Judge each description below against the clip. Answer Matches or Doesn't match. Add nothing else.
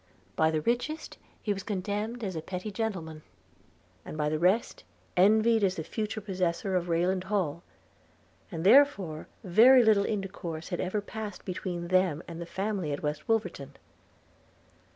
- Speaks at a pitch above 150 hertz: Matches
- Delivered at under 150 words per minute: Doesn't match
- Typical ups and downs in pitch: Matches